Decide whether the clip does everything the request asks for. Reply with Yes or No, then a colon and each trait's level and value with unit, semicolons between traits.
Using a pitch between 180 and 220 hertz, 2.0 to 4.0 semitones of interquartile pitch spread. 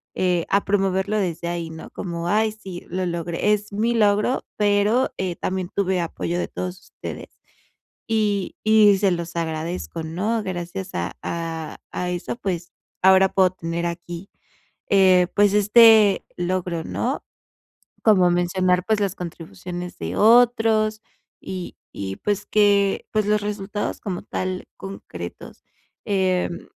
Yes: high, 190 Hz; average, 2.9 semitones